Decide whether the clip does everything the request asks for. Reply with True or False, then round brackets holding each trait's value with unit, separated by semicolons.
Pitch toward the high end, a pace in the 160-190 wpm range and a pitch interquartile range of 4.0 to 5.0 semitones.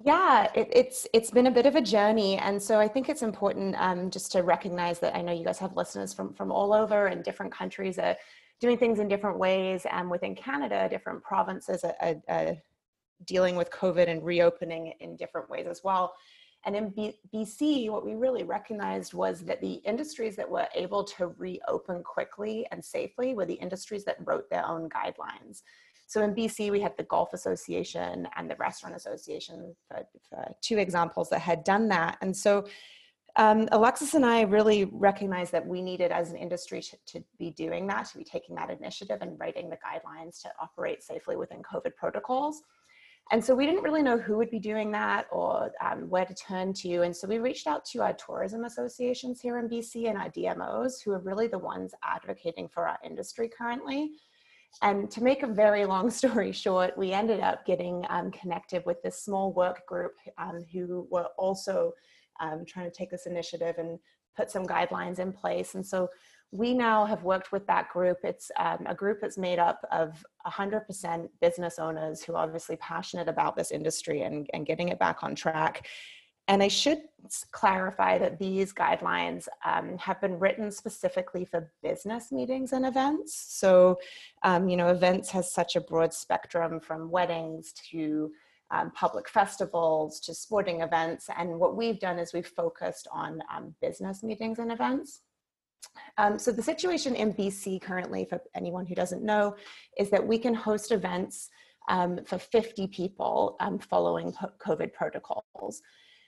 True (195 Hz; 185 wpm; 4.6 semitones)